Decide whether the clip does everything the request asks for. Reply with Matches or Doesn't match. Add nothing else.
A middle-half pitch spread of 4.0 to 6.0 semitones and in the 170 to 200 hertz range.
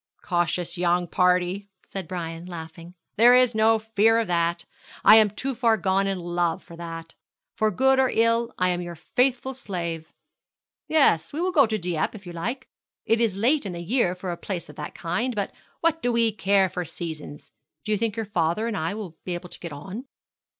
Matches